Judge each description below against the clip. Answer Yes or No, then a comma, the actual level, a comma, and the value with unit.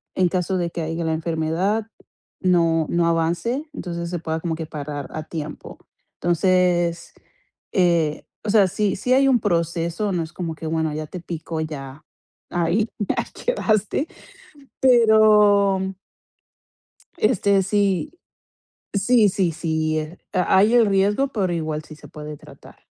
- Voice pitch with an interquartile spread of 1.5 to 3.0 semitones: No, average, 4.0 semitones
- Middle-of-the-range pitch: Yes, medium, 175 Hz